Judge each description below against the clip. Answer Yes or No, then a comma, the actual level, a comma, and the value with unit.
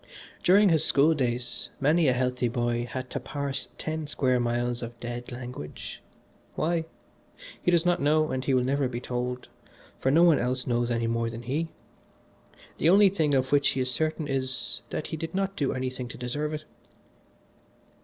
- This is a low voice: Yes, low, 130 Hz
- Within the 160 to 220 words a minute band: Yes, average, 185 wpm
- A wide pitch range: No, average, 4.1 semitones